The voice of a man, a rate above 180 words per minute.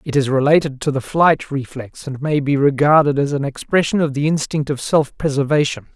Yes: male; average, 200 wpm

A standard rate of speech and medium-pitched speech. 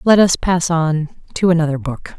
Yes: average, 190 wpm; medium, 165 Hz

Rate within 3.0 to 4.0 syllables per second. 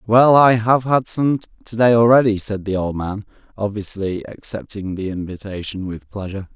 No: 5.0 syllables/s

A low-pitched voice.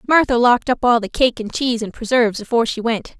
No: high, 235 Hz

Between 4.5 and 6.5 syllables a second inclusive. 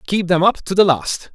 Yes: 5.0 syllables/s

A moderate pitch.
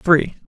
Yes: medium, 165 Hz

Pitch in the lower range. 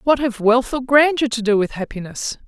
No: high, 245 Hz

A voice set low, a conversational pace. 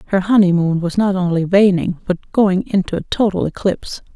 No: medium, 185 Hz; average, 175 wpm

